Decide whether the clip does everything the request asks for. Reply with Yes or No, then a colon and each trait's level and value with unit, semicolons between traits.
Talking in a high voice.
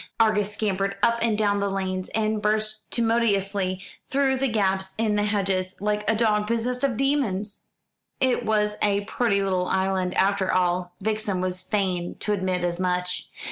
Yes: high, 205 Hz